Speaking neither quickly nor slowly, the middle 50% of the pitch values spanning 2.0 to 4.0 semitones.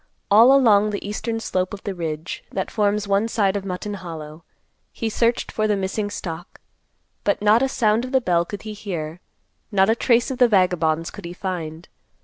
Yes: average, 195 wpm; average, 3.6 semitones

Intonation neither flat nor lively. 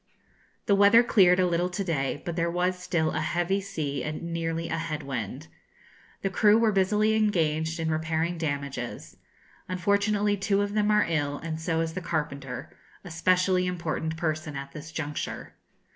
Yes: average, 3.6 semitones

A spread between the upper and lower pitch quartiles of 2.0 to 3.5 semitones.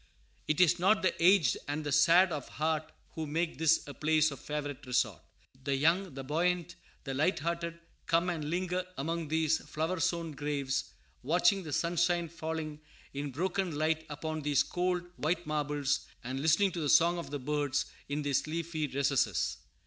Yes: average, 2.8 semitones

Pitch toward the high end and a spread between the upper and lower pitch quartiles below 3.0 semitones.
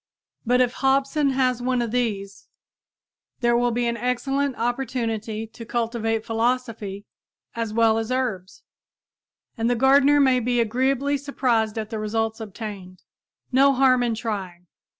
Yes: high, 235 Hz; narrow, 2.5 semitones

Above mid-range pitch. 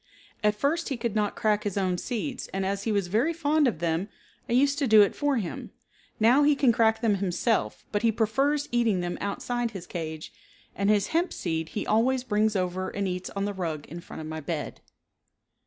Yes: high, 210 Hz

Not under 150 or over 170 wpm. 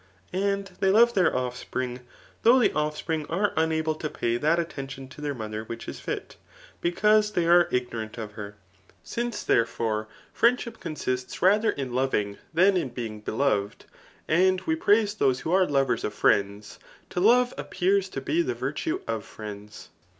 Yes: average, 165 wpm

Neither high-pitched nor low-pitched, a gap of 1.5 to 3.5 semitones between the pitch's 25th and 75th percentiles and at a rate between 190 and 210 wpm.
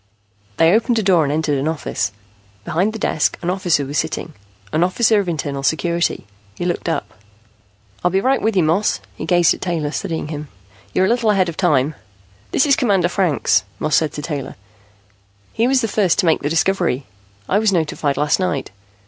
No: medium, 170 Hz; average, 4.4 semitones; average, 195 wpm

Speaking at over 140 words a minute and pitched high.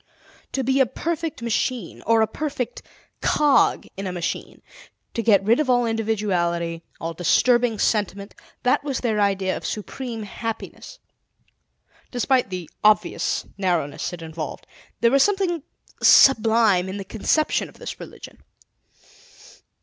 No: slow, 135 wpm; high, 225 Hz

